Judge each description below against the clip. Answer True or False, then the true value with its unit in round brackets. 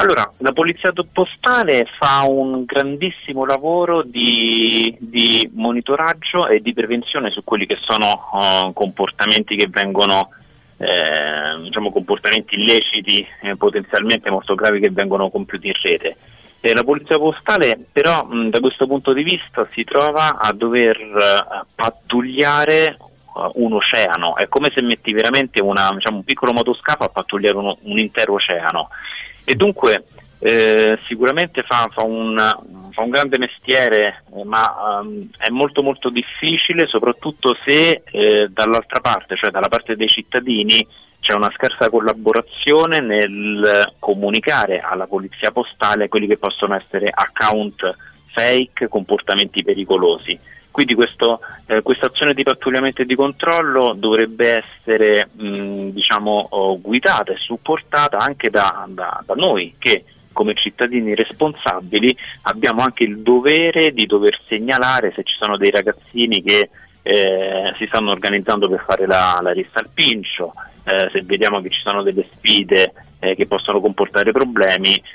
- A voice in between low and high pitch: False (115 Hz)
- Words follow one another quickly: False (140 wpm)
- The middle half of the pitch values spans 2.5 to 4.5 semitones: False (5.0 semitones)